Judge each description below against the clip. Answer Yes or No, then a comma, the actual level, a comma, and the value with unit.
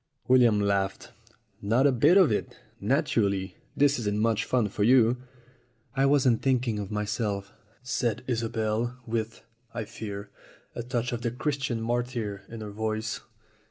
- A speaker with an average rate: Yes, average, 145 wpm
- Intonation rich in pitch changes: No, average, 3.1 semitones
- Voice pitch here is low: Yes, low, 115 Hz